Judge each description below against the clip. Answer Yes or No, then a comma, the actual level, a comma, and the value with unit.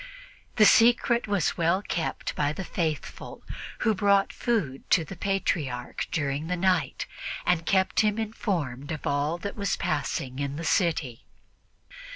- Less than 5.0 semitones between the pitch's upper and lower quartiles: No, wide, 5.5 semitones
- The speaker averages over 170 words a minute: No, average, 145 wpm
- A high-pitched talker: No, medium, 170 Hz